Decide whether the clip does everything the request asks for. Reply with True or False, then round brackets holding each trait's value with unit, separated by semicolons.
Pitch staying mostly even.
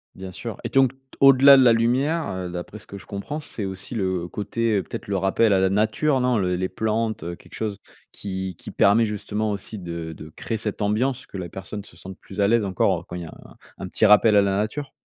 False (3.5 semitones)